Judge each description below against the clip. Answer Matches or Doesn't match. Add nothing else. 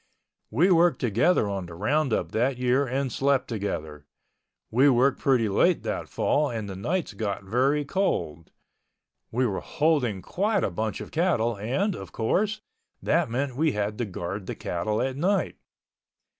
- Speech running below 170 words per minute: Matches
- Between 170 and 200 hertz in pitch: Doesn't match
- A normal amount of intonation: Doesn't match